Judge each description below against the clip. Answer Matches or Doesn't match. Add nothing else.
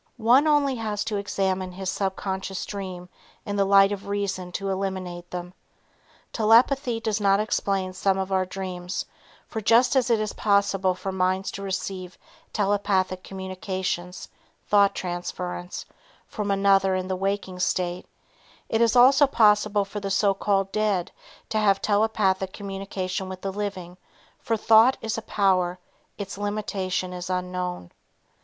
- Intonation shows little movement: Matches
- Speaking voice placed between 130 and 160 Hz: Doesn't match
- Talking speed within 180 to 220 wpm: Doesn't match